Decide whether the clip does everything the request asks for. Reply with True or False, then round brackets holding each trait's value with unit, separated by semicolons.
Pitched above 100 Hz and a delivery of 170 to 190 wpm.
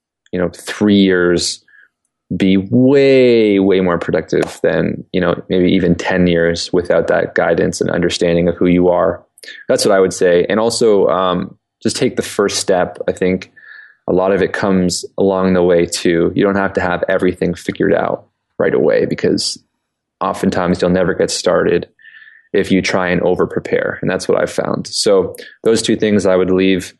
False (95 Hz; 185 wpm)